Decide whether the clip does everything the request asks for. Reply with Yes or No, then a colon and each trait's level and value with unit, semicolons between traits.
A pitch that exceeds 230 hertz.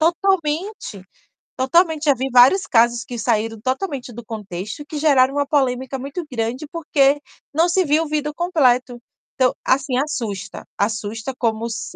Yes: very high, 265 Hz